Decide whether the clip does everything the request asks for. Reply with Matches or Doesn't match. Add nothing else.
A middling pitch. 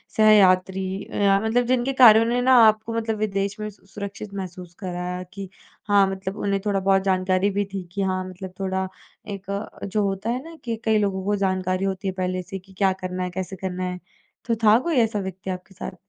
Doesn't match